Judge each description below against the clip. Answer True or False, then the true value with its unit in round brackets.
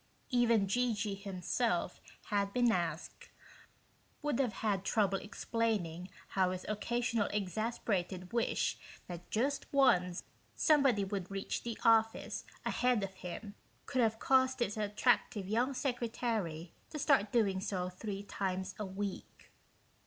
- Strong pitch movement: False (3.9 semitones)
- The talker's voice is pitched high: True (210 Hz)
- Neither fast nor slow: False (130 wpm)